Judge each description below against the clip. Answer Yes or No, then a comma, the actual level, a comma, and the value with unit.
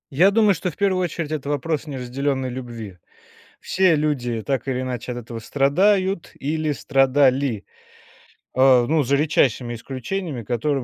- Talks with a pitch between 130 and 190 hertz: Yes, medium, 140 Hz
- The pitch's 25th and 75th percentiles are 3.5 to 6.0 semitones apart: Yes, average, 4.1 semitones